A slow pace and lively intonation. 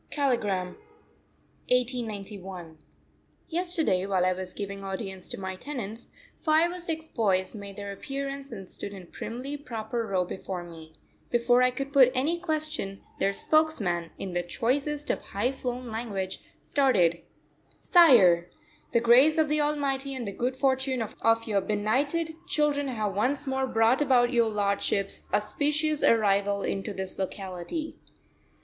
No: average, 145 wpm; wide, 6.0 semitones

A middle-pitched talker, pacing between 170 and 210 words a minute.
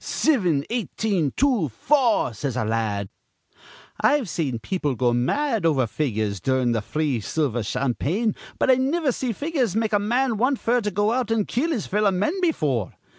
No: high, 195 Hz; average, 175 wpm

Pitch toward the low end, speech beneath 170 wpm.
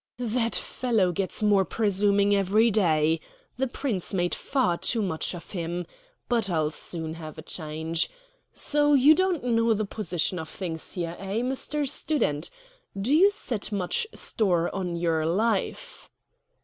No: high, 195 Hz; average, 150 wpm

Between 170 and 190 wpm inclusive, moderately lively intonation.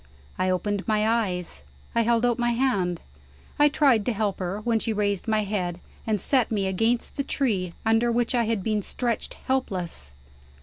Yes: average, 180 wpm; average, 3.6 semitones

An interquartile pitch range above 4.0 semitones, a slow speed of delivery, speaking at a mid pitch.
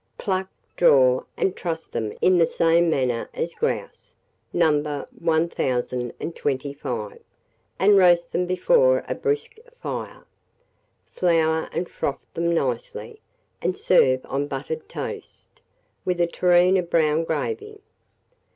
Yes: average, 4.4 semitones; slow, 115 wpm; medium, 170 Hz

